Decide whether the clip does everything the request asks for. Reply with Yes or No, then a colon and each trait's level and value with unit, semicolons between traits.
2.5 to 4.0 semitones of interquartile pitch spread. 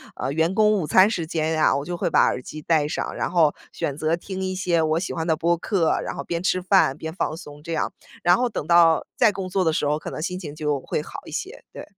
Yes: average, 2.9 semitones